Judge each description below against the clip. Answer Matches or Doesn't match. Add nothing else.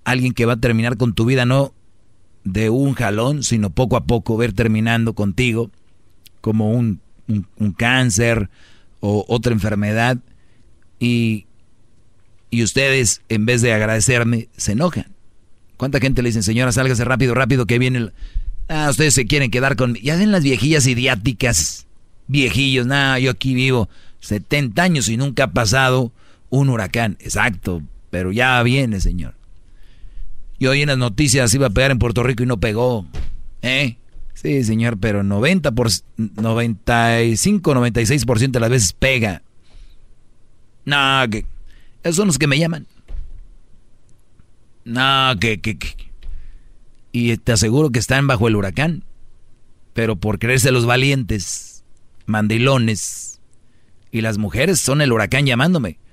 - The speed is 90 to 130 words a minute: Doesn't match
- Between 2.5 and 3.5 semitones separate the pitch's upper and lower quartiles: Matches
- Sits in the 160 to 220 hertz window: Doesn't match